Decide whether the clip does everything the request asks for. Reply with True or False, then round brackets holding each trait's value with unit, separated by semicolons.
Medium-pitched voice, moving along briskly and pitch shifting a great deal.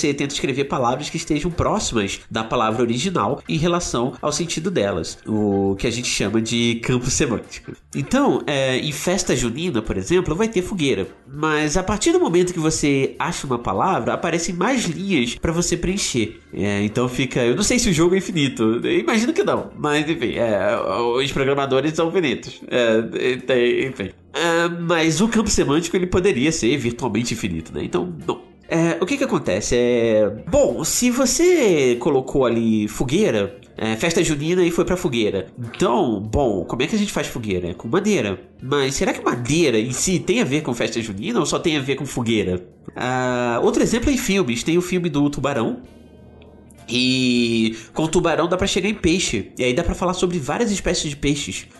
True (145 Hz; 190 wpm; 7.2 semitones)